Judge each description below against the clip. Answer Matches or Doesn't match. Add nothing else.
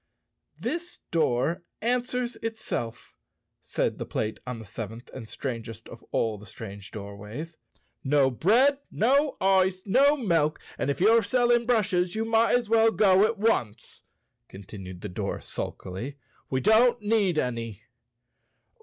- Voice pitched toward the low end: Doesn't match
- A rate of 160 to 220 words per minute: Doesn't match